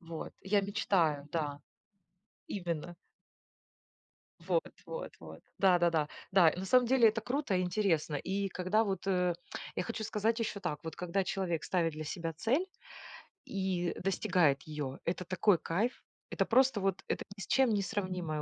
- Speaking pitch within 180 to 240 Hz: Yes, medium, 185 Hz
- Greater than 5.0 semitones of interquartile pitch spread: No, average, 3.8 semitones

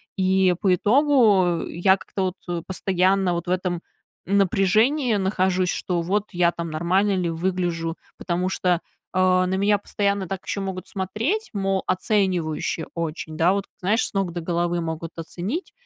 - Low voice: No, medium, 185 Hz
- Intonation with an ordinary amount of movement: No, narrow, 2.2 semitones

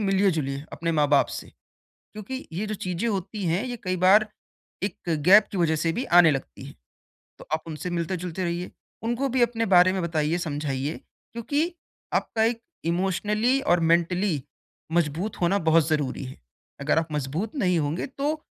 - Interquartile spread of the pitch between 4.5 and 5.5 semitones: Yes, average, 5.0 semitones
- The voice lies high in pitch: No, medium, 180 Hz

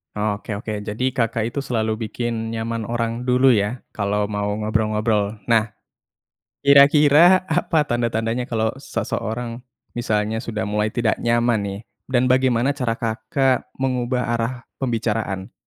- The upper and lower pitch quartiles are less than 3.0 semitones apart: Yes, narrow, 2.6 semitones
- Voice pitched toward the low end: Yes, low, 115 Hz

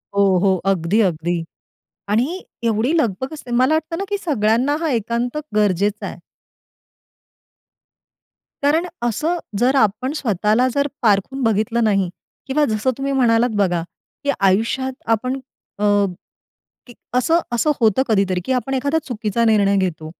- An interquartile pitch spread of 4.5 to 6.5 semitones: Yes, average, 4.8 semitones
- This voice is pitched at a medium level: No, high, 230 Hz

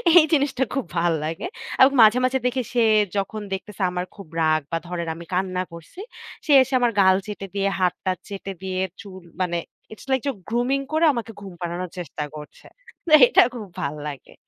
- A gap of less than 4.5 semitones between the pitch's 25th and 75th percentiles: No, wide, 5.6 semitones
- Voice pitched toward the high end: Yes, high, 195 Hz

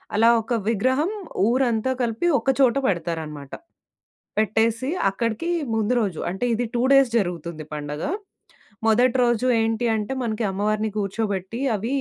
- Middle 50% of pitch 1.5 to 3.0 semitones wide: No, average, 3.6 semitones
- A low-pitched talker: No, high, 220 Hz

